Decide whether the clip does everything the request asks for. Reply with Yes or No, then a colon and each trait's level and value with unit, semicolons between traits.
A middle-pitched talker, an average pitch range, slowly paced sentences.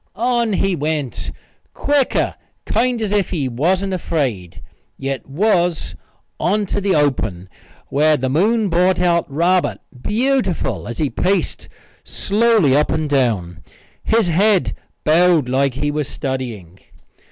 No: medium, 165 Hz; wide, 6.6 semitones; slow, 130 wpm